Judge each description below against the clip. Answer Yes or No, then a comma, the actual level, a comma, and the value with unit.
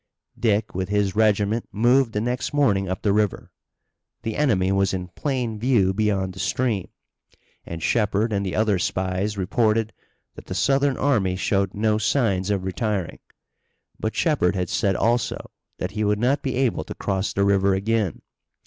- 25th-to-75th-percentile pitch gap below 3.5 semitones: Yes, average, 3.0 semitones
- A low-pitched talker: Yes, low, 105 Hz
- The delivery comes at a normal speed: Yes, average, 165 wpm